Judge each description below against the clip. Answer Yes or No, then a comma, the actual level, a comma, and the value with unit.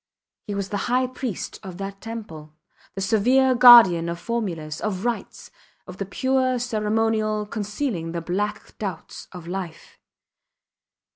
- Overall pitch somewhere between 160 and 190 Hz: No, high, 210 Hz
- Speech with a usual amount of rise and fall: Yes, average, 4.3 semitones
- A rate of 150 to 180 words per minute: No, slow, 135 wpm